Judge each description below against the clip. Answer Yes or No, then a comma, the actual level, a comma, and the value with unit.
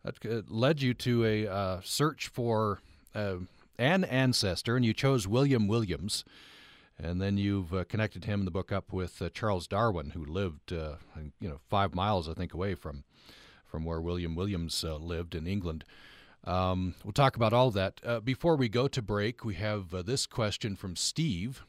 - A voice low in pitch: Yes, low, 100 Hz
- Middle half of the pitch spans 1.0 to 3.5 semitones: No, average, 4.7 semitones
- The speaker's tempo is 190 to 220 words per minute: Yes, average, 195 wpm